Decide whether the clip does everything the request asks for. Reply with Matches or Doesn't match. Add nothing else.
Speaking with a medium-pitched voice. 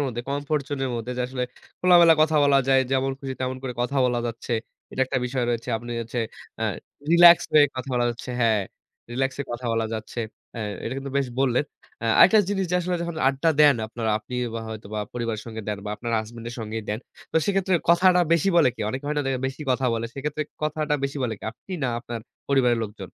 Doesn't match